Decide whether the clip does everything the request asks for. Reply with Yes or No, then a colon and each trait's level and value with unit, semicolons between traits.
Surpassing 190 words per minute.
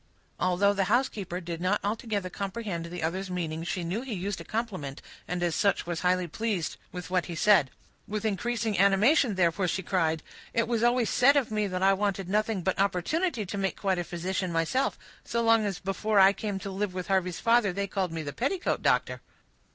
Yes: fast, 205 wpm